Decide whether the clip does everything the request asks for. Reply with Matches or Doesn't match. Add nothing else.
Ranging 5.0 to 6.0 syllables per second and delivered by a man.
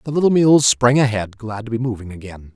Matches